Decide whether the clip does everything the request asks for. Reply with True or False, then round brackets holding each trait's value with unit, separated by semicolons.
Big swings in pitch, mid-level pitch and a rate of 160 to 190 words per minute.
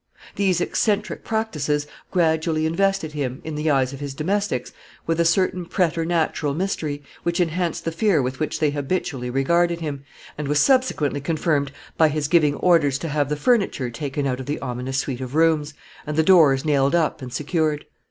False (3.3 semitones; 155 Hz; 180 wpm)